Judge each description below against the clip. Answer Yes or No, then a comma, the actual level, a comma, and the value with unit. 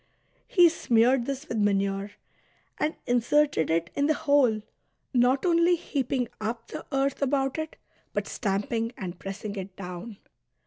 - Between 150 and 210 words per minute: No, average, 140 wpm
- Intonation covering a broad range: Yes, wide, 5.9 semitones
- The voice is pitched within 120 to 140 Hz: No, high, 240 Hz